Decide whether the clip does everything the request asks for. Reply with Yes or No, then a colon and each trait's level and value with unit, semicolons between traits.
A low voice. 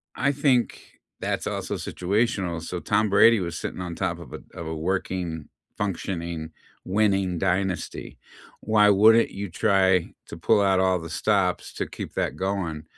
Yes: very low, 95 Hz